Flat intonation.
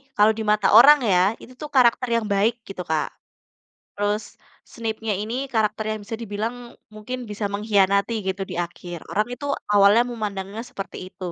Yes: narrow, 2.2 semitones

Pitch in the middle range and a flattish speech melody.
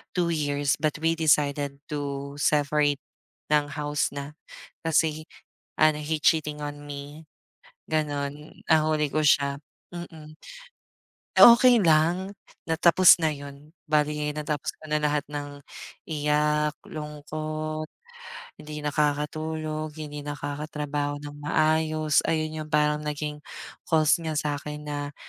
Yes: medium, 150 Hz; narrow, 1.1 semitones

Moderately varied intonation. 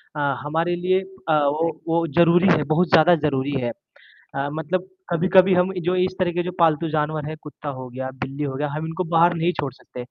Yes: average, 3.1 semitones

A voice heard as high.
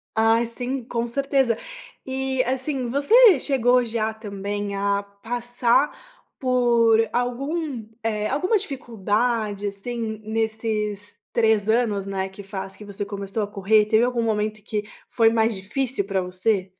Yes: high, 225 Hz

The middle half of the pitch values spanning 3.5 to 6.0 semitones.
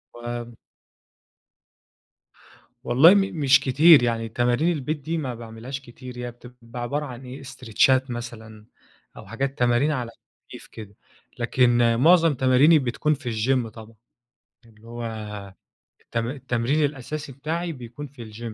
No: average, 3.0 semitones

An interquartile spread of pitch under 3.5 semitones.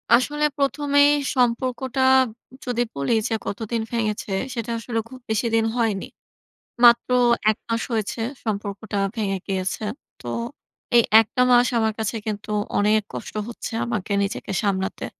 Yes: average, 2.7 semitones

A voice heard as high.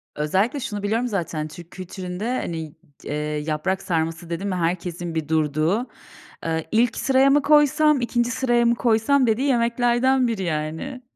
Yes: high, 205 Hz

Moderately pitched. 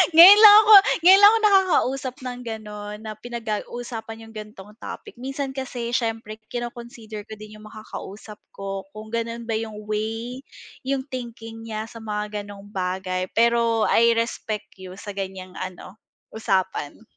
No: high, 225 Hz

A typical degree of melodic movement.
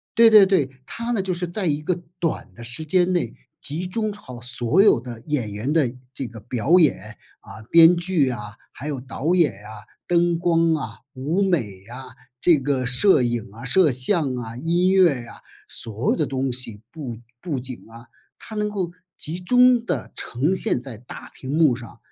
No: wide, 6.4 semitones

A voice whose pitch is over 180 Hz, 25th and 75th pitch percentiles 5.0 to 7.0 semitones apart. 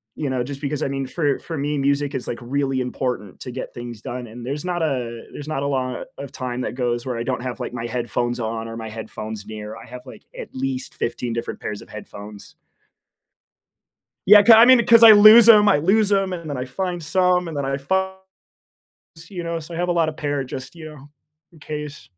No: low, 135 Hz; wide, 5.5 semitones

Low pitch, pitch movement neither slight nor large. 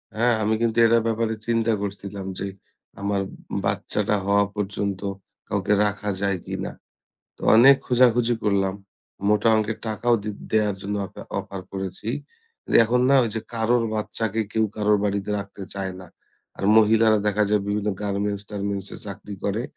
No: low, 105 Hz; narrow, 2.0 semitones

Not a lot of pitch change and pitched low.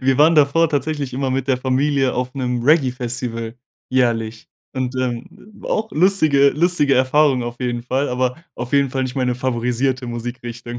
Yes: narrow, 2.3 semitones; low, 130 Hz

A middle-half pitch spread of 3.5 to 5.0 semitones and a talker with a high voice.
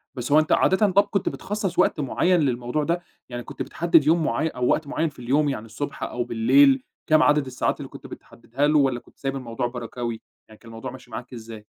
No: average, 4.2 semitones; low, 135 Hz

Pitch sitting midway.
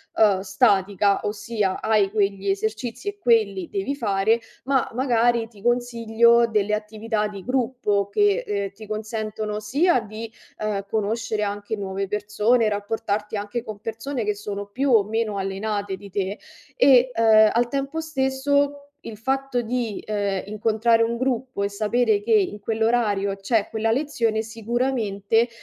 No: high, 220 Hz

